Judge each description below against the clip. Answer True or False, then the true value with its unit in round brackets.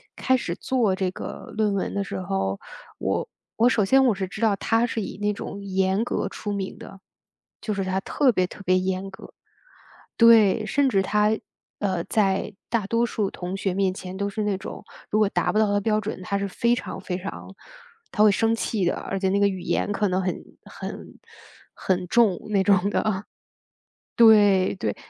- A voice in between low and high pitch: False (200 Hz)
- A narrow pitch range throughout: True (2.3 semitones)